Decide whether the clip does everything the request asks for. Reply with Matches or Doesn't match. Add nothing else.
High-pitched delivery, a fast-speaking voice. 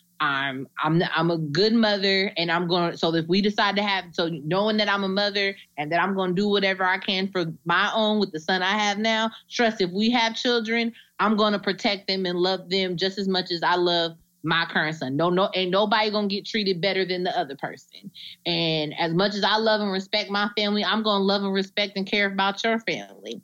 Matches